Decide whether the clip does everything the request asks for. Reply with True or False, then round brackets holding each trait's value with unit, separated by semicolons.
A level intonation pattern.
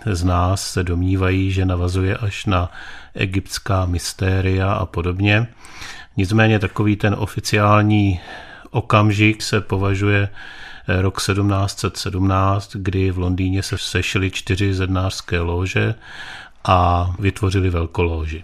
True (1.9 semitones)